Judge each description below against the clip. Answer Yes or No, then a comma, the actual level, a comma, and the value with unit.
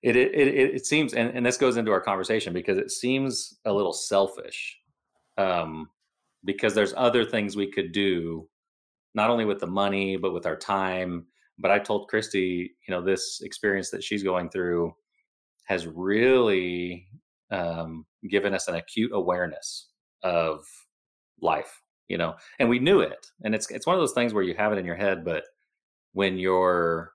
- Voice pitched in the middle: No, low, 100 Hz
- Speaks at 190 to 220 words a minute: No, average, 175 wpm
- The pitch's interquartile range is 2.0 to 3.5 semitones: No, average, 4.8 semitones